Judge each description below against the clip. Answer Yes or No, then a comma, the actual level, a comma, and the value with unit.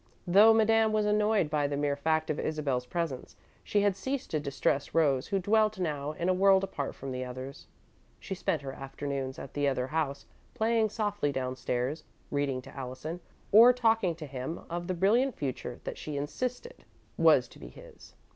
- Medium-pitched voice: Yes, medium, 155 Hz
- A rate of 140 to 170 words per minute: No, average, 185 wpm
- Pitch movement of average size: No, wide, 6.9 semitones